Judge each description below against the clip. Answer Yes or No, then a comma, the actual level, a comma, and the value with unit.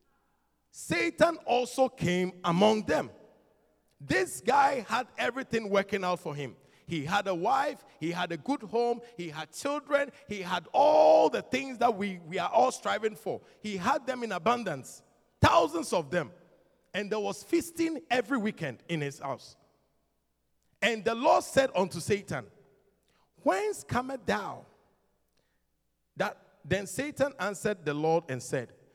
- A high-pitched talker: Yes, high, 205 Hz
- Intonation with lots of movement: Yes, wide, 7.0 semitones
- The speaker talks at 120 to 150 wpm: Yes, average, 145 wpm